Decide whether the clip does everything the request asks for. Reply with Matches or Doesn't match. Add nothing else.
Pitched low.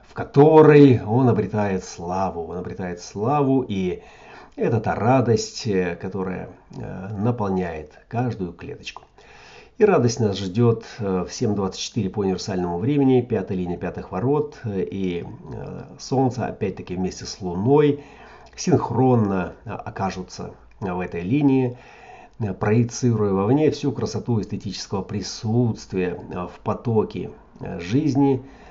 Matches